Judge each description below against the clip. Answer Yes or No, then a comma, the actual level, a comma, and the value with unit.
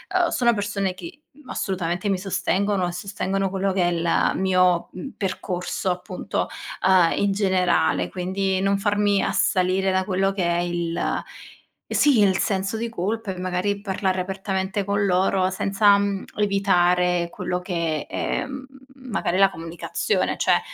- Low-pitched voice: No, high, 190 Hz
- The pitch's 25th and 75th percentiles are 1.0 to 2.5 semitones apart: Yes, narrow, 1.8 semitones